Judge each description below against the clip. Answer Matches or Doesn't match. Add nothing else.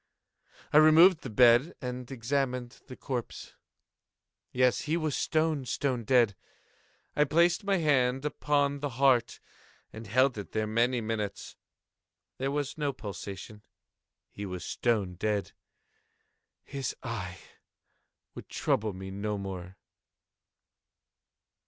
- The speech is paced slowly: Matches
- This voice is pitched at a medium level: Doesn't match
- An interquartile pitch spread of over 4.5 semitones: Matches